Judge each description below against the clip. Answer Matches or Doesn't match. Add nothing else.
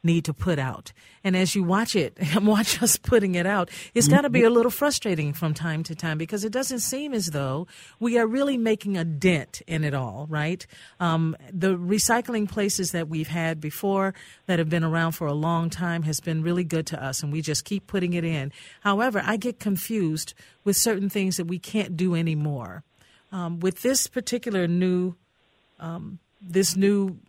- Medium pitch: Matches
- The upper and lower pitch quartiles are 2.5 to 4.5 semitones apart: Matches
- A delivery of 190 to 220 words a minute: Matches